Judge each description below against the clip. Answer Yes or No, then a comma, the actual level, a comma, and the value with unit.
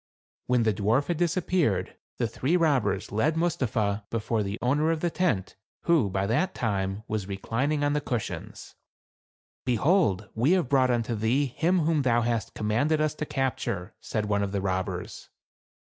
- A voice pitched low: Yes, low, 120 Hz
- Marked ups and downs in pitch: Yes, wide, 6.7 semitones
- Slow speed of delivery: No, average, 170 wpm